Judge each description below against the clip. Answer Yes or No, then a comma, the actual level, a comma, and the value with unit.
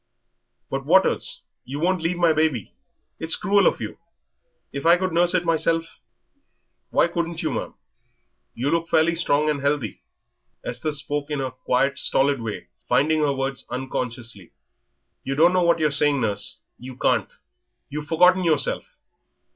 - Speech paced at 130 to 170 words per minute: Yes, average, 155 wpm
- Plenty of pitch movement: No, average, 3.8 semitones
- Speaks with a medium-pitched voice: Yes, medium, 150 Hz